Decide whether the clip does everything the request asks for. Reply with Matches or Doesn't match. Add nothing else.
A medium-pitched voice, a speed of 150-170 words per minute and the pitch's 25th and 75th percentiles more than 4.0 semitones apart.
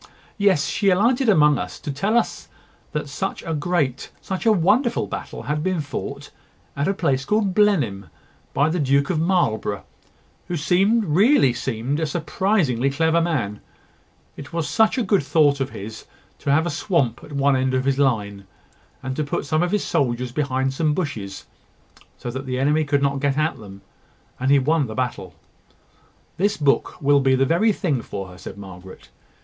Doesn't match